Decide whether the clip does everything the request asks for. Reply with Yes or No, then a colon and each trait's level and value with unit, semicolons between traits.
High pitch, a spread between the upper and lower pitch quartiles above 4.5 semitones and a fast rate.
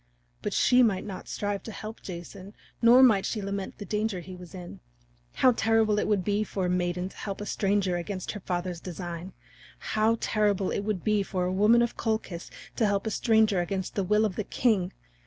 No: high, 200 Hz; average, 2.8 semitones; fast, 210 wpm